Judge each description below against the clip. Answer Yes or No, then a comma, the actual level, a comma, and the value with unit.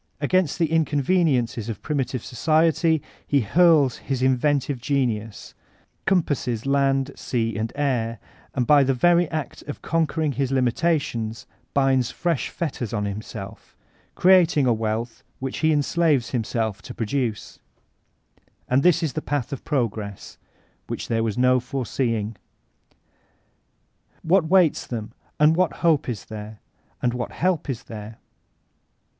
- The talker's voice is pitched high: No, low, 135 Hz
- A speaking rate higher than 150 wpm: No, average, 140 wpm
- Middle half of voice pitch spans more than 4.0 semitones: Yes, average, 5.3 semitones